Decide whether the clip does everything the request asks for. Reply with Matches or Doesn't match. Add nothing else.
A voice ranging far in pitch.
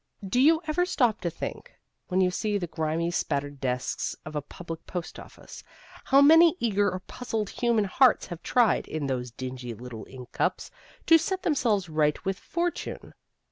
Matches